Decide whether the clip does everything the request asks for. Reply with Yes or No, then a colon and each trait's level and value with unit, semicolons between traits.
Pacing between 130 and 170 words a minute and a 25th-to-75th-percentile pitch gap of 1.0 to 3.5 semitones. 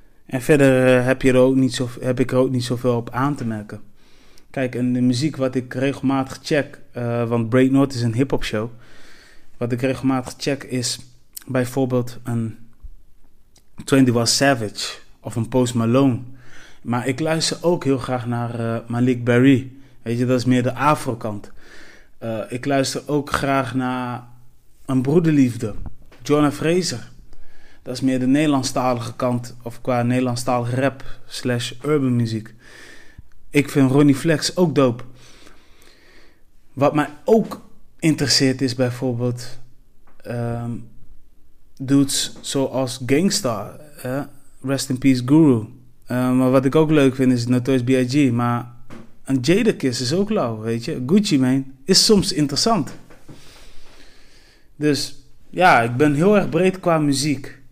Yes: average, 145 wpm; narrow, 2.4 semitones